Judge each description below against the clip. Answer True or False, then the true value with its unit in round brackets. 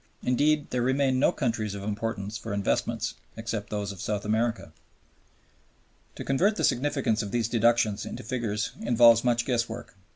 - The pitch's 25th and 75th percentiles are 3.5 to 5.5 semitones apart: False (2.8 semitones)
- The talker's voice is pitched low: True (115 Hz)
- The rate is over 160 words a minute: False (155 wpm)